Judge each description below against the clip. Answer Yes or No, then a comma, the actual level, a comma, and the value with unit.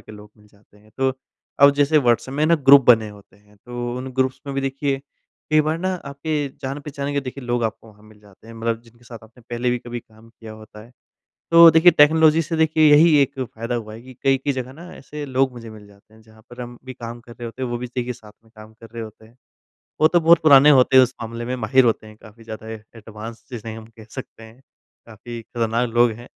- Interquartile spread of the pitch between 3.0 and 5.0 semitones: Yes, average, 3.7 semitones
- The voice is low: Yes, low, 120 Hz